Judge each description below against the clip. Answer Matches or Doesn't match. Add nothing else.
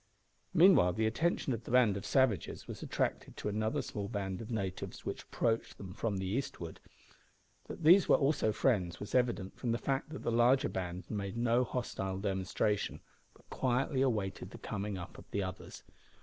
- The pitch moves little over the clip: Doesn't match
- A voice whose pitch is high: Doesn't match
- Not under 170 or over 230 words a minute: Matches